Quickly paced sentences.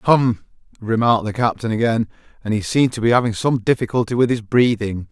No: average, 190 wpm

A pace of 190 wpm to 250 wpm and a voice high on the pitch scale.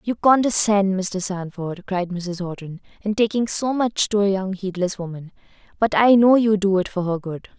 Yes: average, 200 wpm; high, 195 Hz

